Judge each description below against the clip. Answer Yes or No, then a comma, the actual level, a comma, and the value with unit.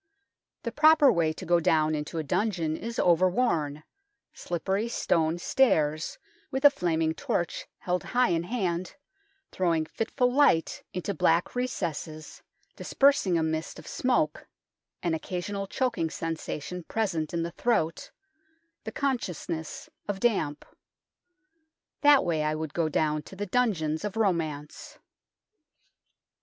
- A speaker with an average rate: No, slow, 130 wpm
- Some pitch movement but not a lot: No, wide, 6.0 semitones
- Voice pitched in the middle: Yes, medium, 175 Hz